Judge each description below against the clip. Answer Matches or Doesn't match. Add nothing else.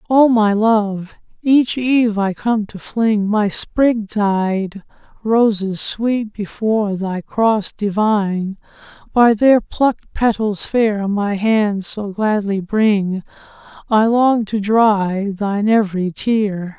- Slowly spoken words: Matches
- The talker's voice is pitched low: Doesn't match